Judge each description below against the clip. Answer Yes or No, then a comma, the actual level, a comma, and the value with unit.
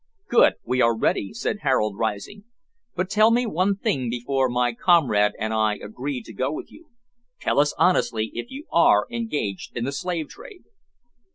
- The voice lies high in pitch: No, low, 135 Hz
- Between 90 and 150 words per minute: No, average, 175 wpm